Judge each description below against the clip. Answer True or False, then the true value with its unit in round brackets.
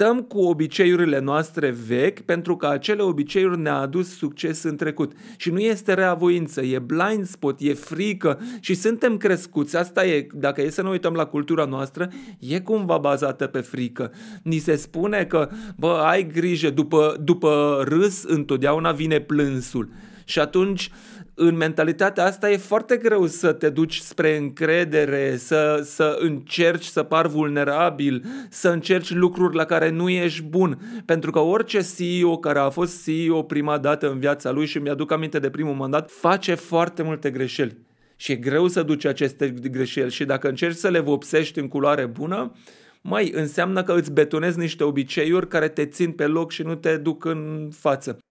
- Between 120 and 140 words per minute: False (170 wpm)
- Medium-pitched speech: True (160 Hz)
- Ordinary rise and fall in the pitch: True (3.4 semitones)